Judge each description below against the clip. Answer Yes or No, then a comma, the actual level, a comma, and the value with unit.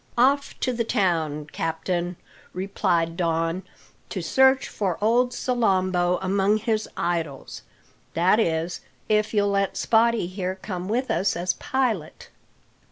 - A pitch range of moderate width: Yes, average, 4.4 semitones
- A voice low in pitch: No, high, 190 Hz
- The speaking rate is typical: No, slow, 125 wpm